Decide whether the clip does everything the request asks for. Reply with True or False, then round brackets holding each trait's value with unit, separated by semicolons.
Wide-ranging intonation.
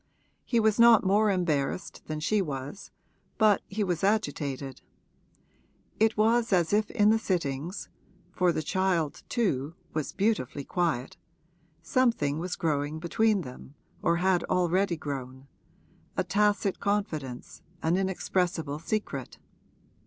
True (5.8 semitones)